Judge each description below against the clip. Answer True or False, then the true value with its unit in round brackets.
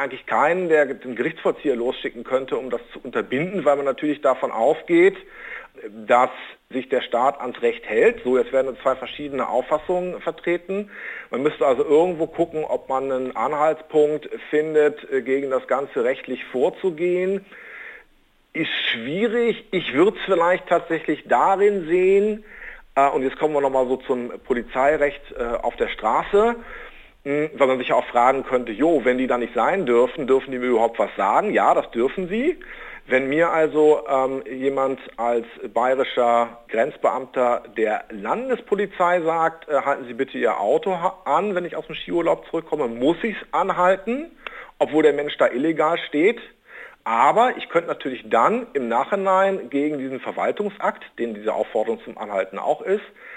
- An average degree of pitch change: False (6.3 semitones)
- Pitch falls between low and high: True (155 Hz)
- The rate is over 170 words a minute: False (160 wpm)